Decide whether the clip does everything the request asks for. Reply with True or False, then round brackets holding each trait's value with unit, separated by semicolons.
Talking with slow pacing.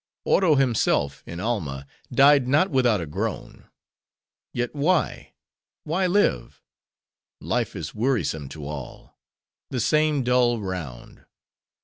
True (110 wpm)